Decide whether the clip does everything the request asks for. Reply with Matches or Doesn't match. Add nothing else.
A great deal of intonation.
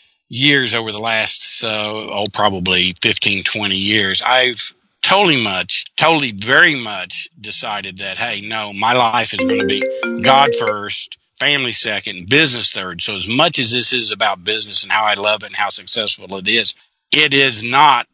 Doesn't match